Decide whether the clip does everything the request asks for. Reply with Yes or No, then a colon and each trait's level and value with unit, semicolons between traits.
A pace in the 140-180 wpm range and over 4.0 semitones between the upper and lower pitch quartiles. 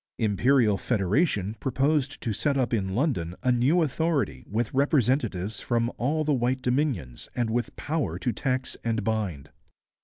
Yes: average, 150 wpm; average, 4.5 semitones